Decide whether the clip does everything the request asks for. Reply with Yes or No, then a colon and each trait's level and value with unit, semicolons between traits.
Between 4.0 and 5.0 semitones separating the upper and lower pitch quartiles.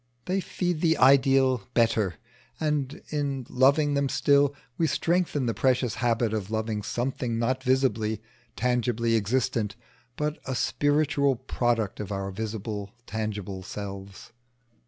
Yes: average, 4.4 semitones